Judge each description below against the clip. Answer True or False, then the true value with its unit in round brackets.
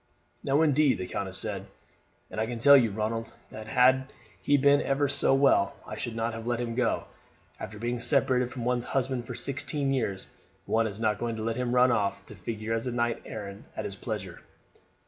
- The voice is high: False (120 Hz)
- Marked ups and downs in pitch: False (3.0 semitones)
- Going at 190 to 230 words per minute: True (205 wpm)